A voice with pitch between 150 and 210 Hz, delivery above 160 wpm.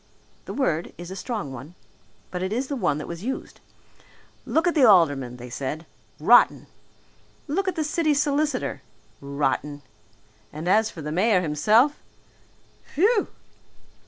No: high, 190 Hz; average, 145 wpm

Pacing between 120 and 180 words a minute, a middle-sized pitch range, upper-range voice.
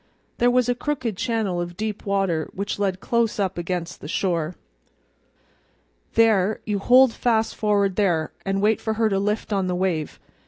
Yes: average, 170 wpm; average, 3.3 semitones; high, 200 Hz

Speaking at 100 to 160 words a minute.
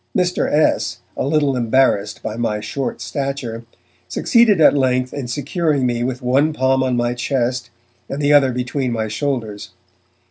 Yes: average, 155 wpm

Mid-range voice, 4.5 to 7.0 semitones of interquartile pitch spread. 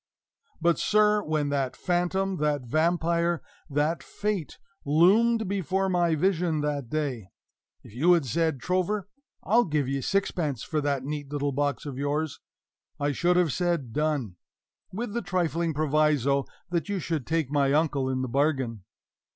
No: medium, 155 Hz; average, 3.9 semitones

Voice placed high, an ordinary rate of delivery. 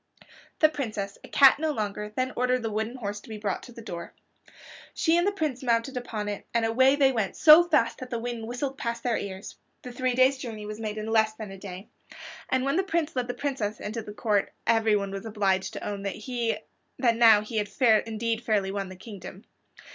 No: high, 225 Hz; fast, 215 wpm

